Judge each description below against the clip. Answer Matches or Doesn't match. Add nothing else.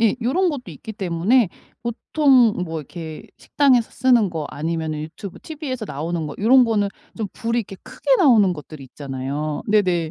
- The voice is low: Doesn't match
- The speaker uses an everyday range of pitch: Doesn't match